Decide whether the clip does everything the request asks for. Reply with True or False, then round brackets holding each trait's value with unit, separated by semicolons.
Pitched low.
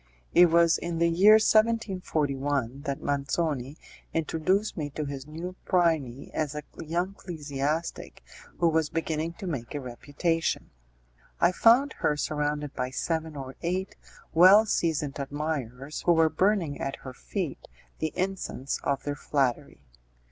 False (155 Hz)